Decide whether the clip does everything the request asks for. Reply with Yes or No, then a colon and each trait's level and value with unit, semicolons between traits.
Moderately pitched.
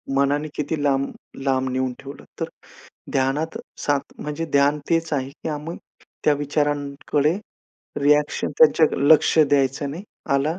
Yes: medium, 145 Hz